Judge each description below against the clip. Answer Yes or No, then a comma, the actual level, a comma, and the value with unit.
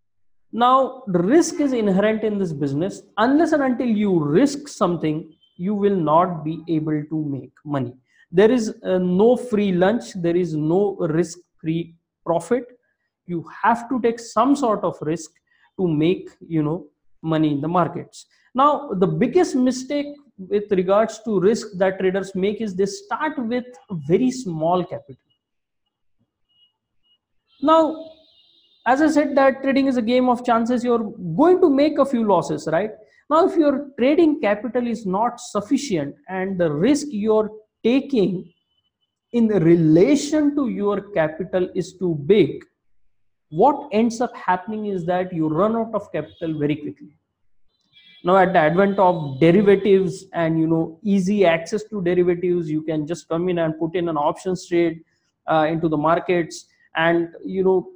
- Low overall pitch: No, high, 190 Hz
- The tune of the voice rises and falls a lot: Yes, wide, 6.3 semitones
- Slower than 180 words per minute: Yes, average, 160 wpm